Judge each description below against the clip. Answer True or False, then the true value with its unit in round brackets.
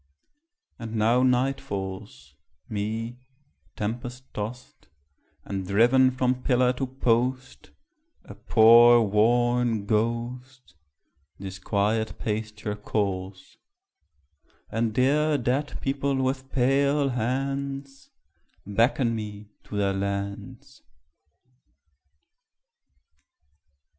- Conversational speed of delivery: False (85 wpm)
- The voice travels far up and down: False (3.7 semitones)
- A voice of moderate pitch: False (120 Hz)